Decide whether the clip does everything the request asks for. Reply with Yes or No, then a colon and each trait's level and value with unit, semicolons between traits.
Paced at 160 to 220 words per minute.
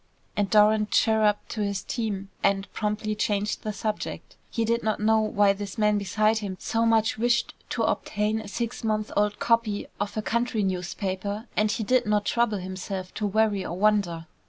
Yes: average, 180 wpm